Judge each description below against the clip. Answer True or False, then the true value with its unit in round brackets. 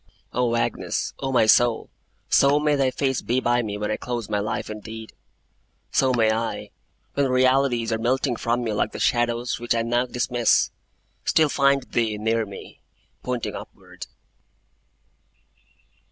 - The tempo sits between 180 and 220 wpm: False (155 wpm)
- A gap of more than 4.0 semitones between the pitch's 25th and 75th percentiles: False (2.4 semitones)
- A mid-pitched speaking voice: False (120 Hz)